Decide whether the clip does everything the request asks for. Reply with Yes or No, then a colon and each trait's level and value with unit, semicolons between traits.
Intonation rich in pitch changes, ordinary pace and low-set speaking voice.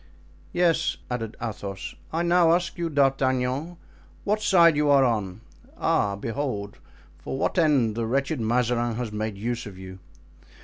Yes: wide, 6.1 semitones; average, 145 wpm; low, 125 Hz